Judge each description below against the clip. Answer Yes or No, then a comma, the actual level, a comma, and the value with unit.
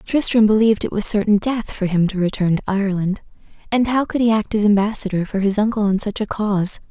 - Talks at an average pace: No, fast, 225 wpm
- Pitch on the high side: Yes, high, 205 Hz